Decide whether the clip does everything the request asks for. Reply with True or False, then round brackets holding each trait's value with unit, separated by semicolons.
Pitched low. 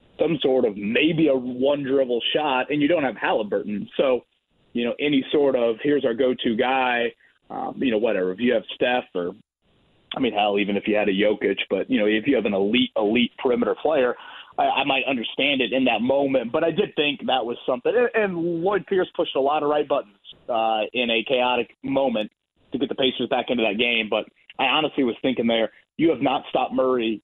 True (130 Hz)